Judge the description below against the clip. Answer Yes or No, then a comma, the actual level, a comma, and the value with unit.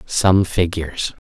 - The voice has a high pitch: No, very low, 90 Hz